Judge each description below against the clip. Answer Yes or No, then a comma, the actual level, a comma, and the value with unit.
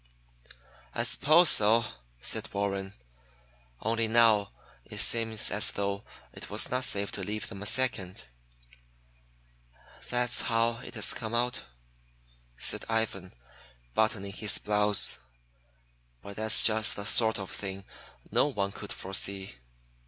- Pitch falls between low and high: No, low, 105 Hz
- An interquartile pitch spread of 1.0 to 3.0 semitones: Yes, narrow, 2.5 semitones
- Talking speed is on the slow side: Yes, slow, 125 wpm